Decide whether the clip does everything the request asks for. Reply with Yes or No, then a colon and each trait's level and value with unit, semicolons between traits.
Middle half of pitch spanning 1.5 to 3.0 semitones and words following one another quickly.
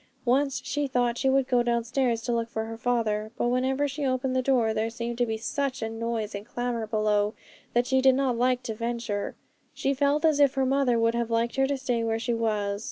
Yes: narrow, 2.6 semitones; fast, 230 wpm